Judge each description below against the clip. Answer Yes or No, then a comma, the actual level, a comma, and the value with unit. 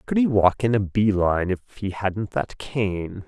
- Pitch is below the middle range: Yes, low, 105 Hz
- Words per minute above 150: Yes, average, 200 wpm